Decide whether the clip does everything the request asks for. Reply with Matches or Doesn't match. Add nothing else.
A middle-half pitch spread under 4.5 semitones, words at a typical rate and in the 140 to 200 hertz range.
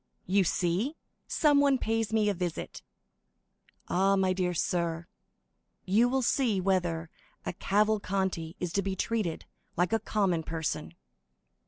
Doesn't match